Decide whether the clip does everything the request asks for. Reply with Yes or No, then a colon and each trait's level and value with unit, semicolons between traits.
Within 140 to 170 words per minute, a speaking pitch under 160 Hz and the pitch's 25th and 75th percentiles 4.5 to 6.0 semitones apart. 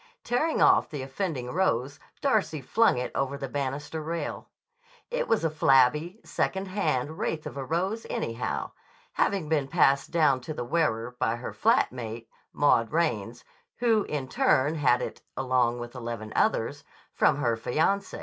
Yes: average, 160 wpm; medium, 140 Hz; average, 5.3 semitones